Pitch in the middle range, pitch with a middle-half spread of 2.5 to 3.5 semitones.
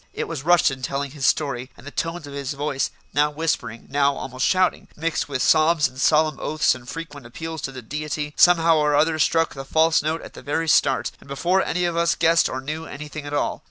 Yes: medium, 150 Hz; average, 2.8 semitones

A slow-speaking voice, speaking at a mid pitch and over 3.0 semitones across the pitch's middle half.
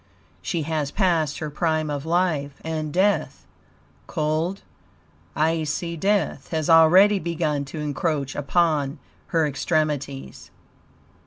No: slow, 105 wpm; medium, 155 Hz; narrow, 2.6 semitones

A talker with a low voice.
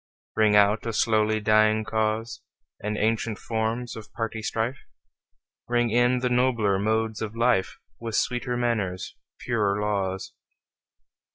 Yes: low, 110 Hz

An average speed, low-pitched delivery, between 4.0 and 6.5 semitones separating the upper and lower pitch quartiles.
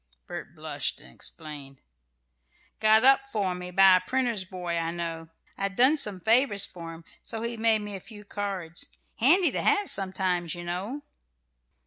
No: average, 165 wpm; high, 195 Hz; average, 4.7 semitones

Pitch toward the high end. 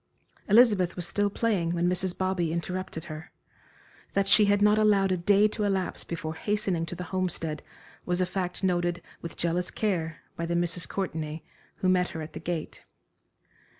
No: medium, 180 Hz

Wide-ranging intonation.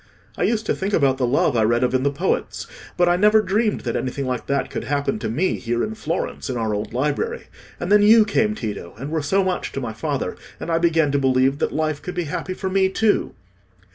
Yes: wide, 6.8 semitones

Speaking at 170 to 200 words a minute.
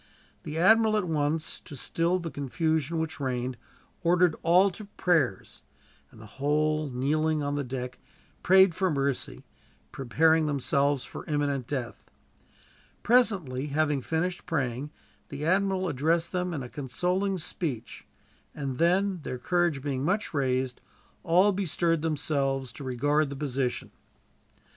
No: slow, 135 wpm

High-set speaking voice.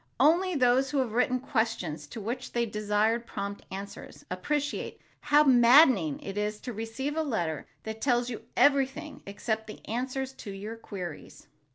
Yes: high, 235 Hz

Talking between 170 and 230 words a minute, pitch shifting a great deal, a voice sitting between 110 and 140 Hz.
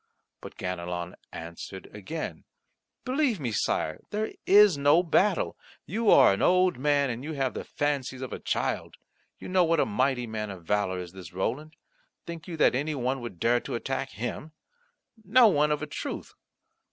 Yes: average, 175 wpm; wide, 7.9 semitones; low, 135 Hz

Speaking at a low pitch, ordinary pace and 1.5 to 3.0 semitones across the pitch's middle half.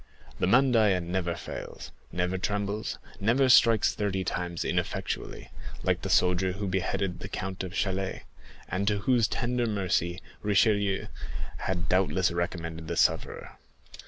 No: very low, 95 Hz; slow, 130 wpm; narrow, 2.5 semitones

